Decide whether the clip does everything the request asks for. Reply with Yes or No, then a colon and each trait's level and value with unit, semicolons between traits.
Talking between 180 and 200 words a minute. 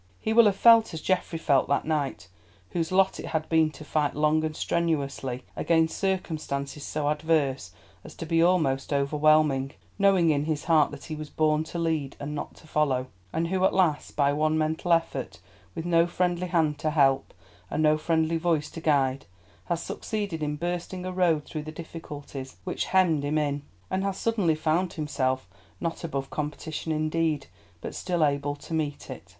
Yes: average, 185 wpm